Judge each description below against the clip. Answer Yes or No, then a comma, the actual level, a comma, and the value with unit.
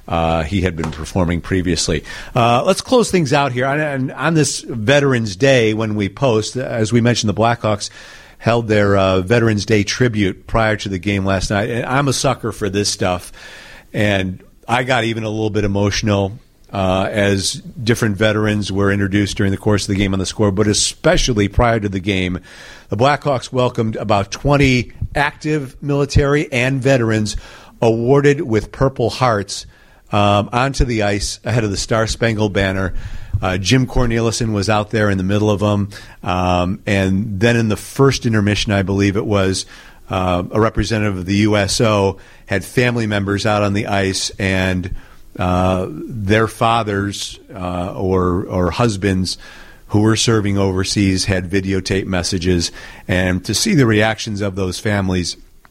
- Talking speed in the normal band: Yes, average, 165 wpm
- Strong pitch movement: No, average, 3.4 semitones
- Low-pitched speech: Yes, low, 105 Hz